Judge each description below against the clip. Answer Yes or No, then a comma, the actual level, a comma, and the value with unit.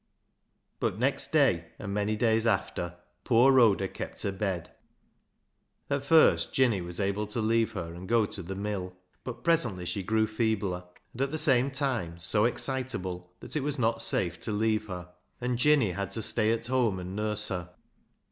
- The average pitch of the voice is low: Yes, low, 110 Hz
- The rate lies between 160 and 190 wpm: Yes, average, 180 wpm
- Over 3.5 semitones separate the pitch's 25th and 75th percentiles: Yes, average, 4.3 semitones